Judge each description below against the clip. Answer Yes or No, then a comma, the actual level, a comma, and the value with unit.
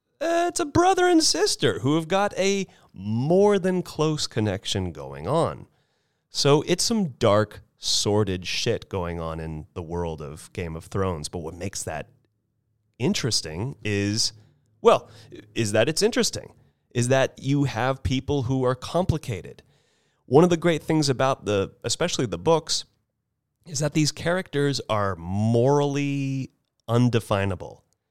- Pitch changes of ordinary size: No, wide, 7.2 semitones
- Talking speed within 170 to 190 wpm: No, average, 145 wpm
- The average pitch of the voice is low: Yes, low, 125 Hz